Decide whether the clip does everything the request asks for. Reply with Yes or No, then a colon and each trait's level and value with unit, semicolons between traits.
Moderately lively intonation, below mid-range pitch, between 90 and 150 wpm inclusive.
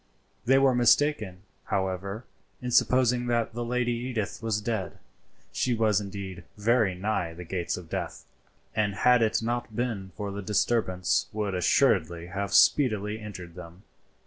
Yes: average, 4.1 semitones; low, 105 Hz; average, 145 wpm